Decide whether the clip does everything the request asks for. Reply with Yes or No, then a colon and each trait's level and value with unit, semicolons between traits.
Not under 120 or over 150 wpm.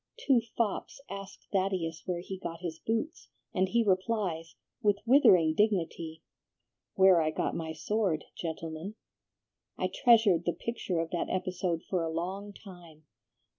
Yes: average, 140 wpm